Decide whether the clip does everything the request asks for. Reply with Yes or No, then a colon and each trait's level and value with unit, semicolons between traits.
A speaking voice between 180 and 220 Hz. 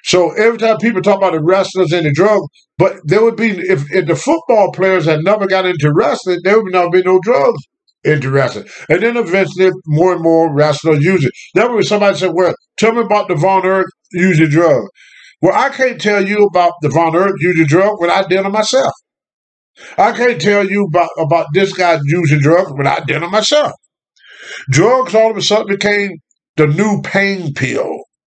Yes: high, 190 Hz